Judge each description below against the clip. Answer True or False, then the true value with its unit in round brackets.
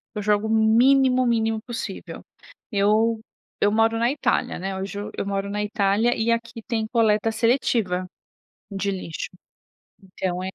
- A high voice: True (220 Hz)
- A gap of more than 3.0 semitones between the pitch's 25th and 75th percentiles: False (2.6 semitones)